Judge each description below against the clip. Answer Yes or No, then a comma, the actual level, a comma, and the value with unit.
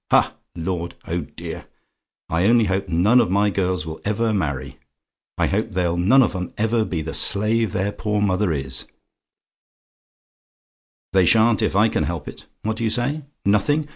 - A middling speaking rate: Yes, average, 170 wpm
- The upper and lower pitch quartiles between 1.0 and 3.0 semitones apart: No, average, 4.2 semitones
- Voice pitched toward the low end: Yes, low, 100 Hz